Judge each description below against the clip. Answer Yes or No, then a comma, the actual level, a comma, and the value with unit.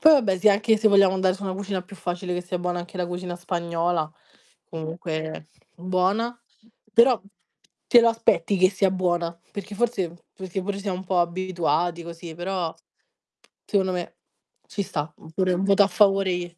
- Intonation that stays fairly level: Yes, narrow, 2.3 semitones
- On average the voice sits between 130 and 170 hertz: No, medium, 185 Hz